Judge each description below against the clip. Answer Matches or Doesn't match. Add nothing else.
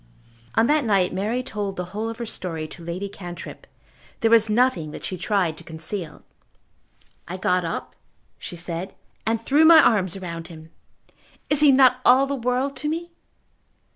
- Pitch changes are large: Matches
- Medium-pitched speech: Doesn't match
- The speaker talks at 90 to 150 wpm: Doesn't match